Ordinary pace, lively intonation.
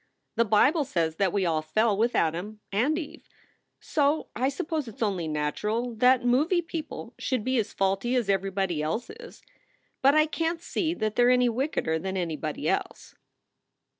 Yes: average, 180 wpm; wide, 6.5 semitones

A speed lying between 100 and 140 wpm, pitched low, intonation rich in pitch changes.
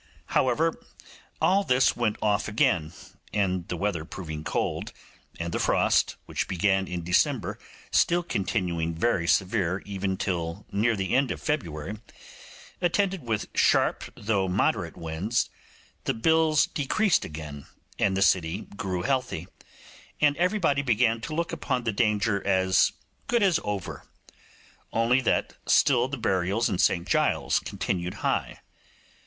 Yes: slow, 135 wpm; low, 105 Hz; wide, 6.2 semitones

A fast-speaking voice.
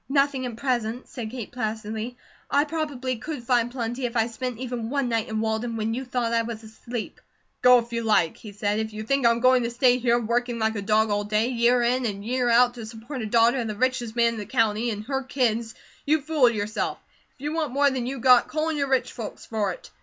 Yes: fast, 245 wpm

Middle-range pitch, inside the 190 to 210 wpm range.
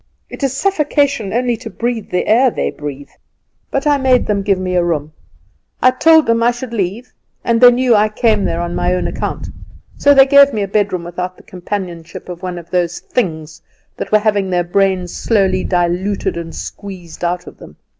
No: high, 200 Hz; average, 195 wpm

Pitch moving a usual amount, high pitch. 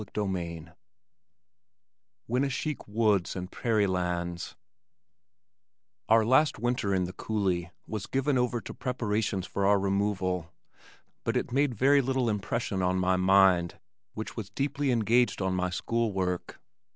No: average, 4.6 semitones; low, 105 Hz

